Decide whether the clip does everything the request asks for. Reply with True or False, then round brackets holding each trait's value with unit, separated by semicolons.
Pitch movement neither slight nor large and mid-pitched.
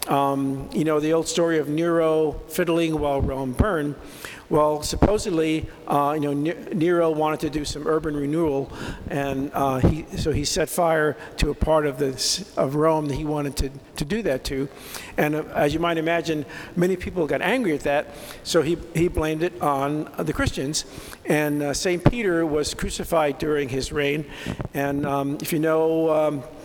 False (2.0 semitones; 155 Hz)